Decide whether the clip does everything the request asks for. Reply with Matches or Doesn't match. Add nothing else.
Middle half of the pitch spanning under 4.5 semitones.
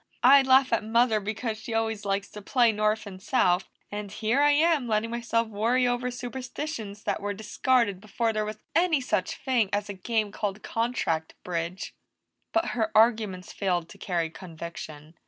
Matches